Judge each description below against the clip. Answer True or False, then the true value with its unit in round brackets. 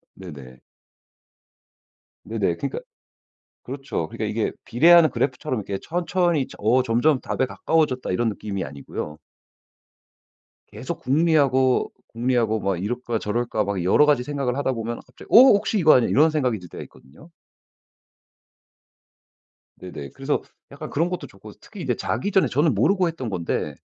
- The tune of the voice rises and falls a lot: True (6.5 semitones)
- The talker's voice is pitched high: False (125 Hz)